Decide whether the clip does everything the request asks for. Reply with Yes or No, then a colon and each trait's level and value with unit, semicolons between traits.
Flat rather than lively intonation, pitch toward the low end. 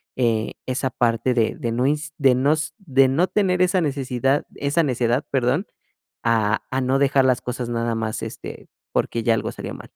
No: average, 3.3 semitones; low, 130 Hz